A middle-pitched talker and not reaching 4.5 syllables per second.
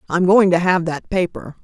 No: medium, 180 Hz; 5.0 syllables/s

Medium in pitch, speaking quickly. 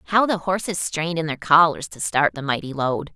Yes: medium, 160 Hz; fast, 230 wpm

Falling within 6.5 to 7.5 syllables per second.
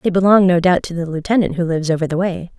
Yes: 7.0 syllables/s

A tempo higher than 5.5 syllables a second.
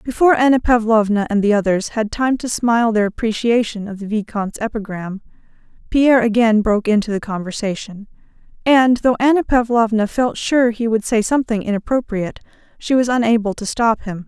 Yes: 5.7 syllables/s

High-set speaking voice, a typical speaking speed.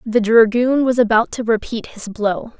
Yes: high, 225 Hz; average, 185 wpm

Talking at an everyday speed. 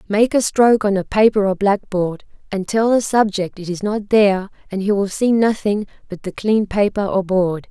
No: fast, 210 wpm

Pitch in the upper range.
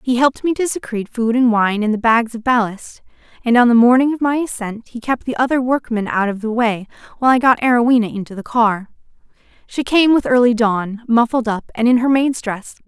Yes: high, 240 Hz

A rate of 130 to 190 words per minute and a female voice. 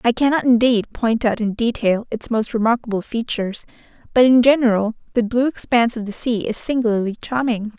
Yes: average, 175 wpm; female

